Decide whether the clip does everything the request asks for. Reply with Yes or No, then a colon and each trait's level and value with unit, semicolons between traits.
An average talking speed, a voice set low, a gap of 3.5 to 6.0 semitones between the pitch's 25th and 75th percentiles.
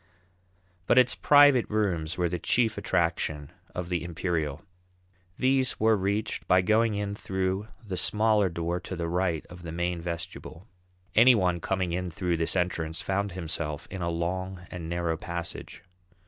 No: average, 160 wpm; very low, 90 Hz; average, 3.1 semitones